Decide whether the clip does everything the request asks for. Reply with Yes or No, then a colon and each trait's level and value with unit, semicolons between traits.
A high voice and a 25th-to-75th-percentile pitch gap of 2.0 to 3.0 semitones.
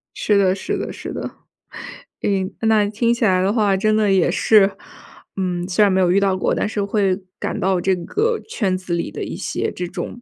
Yes: high, 195 Hz; narrow, 2.4 semitones